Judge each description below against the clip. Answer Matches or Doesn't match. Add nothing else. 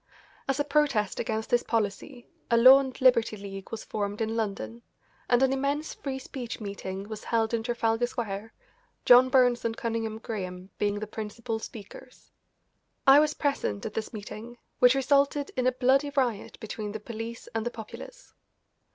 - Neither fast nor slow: Matches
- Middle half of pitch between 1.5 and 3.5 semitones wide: Matches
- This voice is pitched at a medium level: Doesn't match